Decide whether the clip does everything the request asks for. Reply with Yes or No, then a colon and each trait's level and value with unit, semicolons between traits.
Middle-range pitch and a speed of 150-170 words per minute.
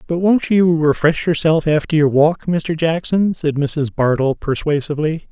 Yes: medium, 155 Hz; average, 160 wpm